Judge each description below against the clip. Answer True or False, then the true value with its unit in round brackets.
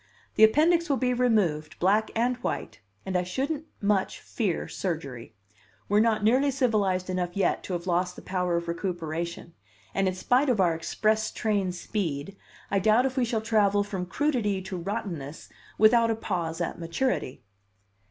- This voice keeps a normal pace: True (165 wpm)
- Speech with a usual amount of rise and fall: True (4.5 semitones)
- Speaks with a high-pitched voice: True (200 Hz)